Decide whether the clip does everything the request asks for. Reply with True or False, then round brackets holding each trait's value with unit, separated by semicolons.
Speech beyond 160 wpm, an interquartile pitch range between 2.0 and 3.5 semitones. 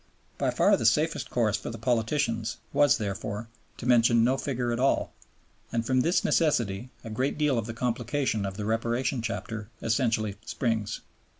True (170 wpm; 2.5 semitones)